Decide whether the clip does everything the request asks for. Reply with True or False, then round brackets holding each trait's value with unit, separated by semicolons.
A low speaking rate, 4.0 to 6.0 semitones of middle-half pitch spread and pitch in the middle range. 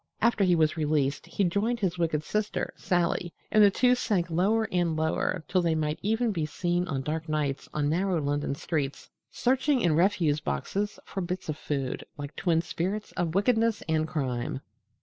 False (180 wpm; 4.7 semitones; 170 Hz)